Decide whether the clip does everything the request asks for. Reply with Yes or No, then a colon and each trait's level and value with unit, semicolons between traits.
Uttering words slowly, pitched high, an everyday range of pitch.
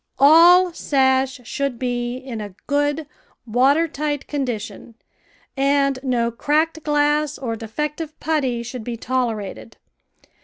Yes: slow, 120 wpm; very high, 270 Hz; average, 3.6 semitones